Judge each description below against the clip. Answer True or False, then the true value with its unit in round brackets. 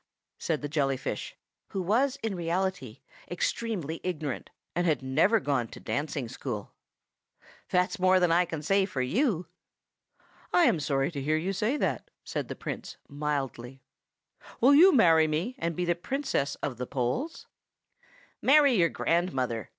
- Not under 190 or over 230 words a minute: False (150 wpm)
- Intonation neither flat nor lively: False (5.7 semitones)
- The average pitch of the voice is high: False (170 Hz)